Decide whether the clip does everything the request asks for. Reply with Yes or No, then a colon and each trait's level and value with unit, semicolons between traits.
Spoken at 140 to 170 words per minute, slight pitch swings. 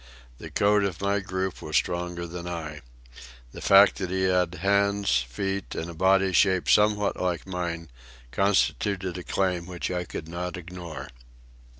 Yes: average, 160 wpm; narrow, 2.1 semitones